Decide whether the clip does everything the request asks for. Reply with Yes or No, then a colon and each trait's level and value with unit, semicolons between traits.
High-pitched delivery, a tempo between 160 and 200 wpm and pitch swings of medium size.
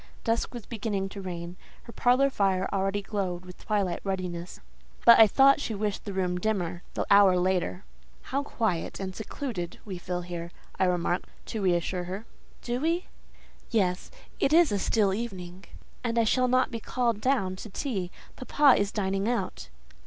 Yes: high, 200 Hz; average, 170 wpm; average, 4.3 semitones